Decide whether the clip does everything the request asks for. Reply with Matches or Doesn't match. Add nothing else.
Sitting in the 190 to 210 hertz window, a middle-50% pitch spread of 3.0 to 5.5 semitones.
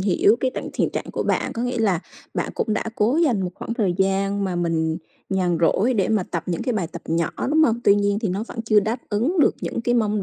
Matches